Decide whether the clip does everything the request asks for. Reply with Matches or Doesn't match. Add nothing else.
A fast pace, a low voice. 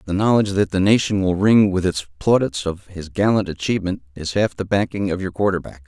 Matches